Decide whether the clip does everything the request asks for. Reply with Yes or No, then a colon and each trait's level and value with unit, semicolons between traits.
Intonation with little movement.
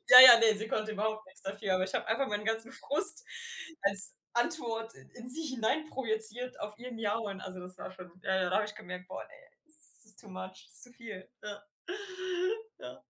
No: average, 3.6 semitones